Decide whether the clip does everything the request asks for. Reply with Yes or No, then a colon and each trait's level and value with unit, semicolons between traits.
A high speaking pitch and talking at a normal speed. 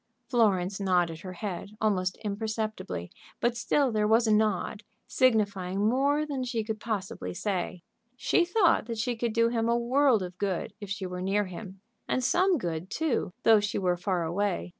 Yes: high, 210 Hz; average, 180 wpm